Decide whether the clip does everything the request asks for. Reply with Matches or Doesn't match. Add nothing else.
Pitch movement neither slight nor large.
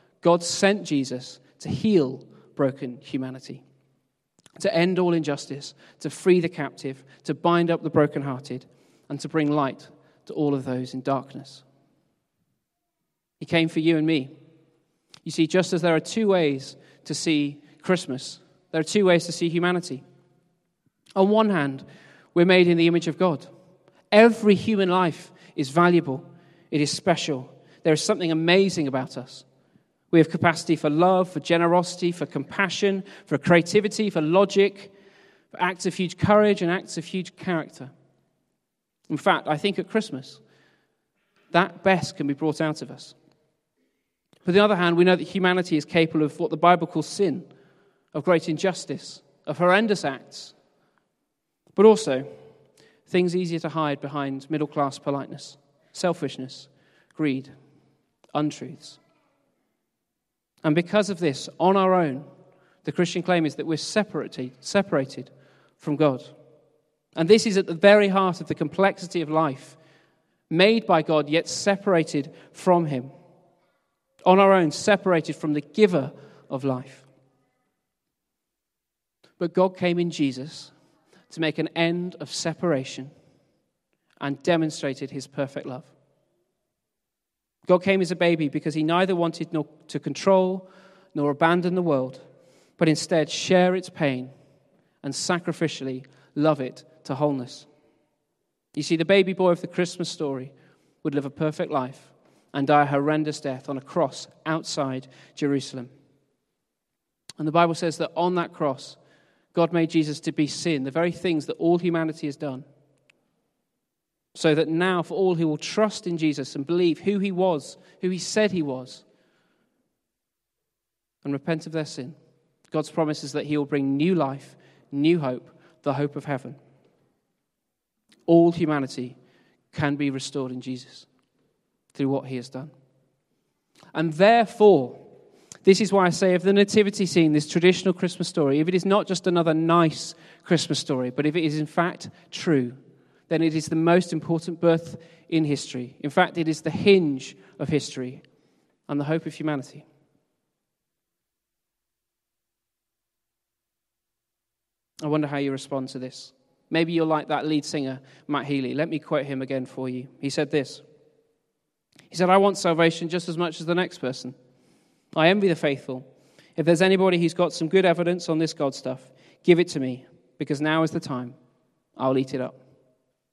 Matches